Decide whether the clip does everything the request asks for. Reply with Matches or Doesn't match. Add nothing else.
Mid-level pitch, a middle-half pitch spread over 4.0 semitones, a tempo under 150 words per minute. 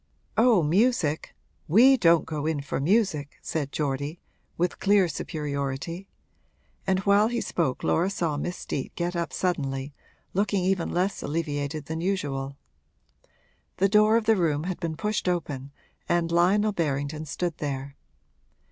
Matches